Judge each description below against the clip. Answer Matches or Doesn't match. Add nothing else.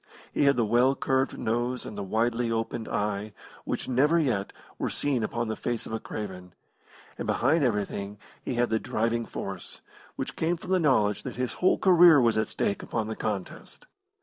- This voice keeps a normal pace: Matches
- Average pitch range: Matches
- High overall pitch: Doesn't match